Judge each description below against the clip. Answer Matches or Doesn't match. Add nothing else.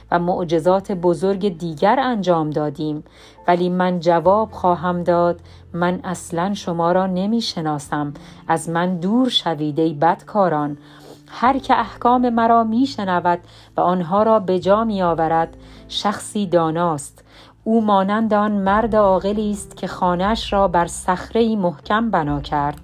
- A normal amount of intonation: Matches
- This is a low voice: Doesn't match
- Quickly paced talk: Doesn't match